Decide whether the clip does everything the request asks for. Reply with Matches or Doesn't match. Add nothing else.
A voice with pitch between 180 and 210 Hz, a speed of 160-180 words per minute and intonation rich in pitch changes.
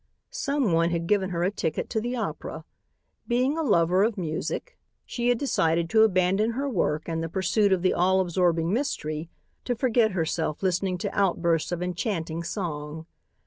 Doesn't match